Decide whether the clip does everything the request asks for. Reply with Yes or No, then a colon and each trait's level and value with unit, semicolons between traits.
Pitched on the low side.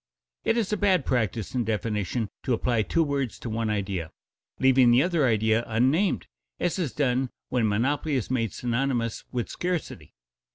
Yes: low, 125 Hz